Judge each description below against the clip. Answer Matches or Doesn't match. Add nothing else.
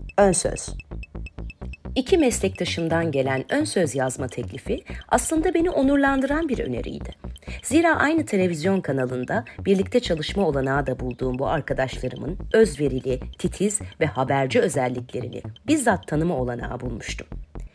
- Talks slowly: Doesn't match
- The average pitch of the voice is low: Doesn't match